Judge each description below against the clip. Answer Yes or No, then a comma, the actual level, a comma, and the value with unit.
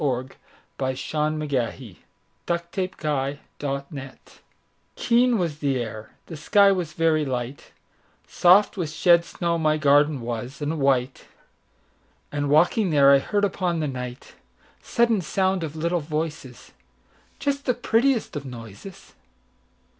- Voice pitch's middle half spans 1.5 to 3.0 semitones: No, average, 4.8 semitones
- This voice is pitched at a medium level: Yes, medium, 150 Hz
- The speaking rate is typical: No, slow, 115 wpm